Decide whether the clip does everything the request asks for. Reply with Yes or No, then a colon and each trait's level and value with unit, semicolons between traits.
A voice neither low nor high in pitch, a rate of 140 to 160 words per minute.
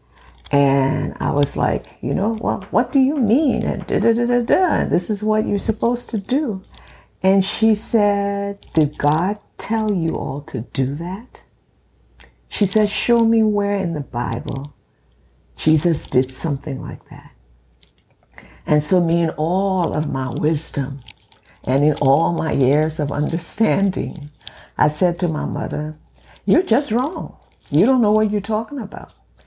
Yes: medium, 160 Hz; average, 150 wpm